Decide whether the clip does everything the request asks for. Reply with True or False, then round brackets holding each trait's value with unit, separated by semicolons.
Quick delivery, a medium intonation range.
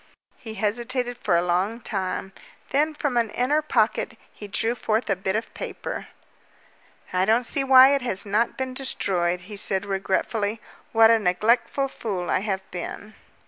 False (165 wpm; 4.2 semitones)